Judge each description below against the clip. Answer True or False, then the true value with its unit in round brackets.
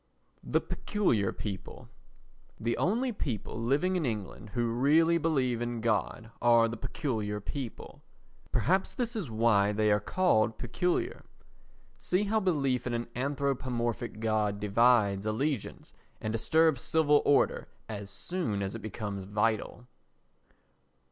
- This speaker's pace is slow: True (125 wpm)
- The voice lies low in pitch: True (120 Hz)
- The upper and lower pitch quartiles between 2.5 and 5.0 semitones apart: False (5.5 semitones)